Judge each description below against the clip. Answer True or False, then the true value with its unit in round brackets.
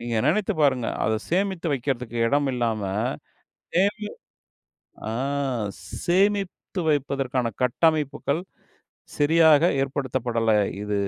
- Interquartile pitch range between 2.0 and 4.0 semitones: False (5.5 semitones)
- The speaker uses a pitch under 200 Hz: True (140 Hz)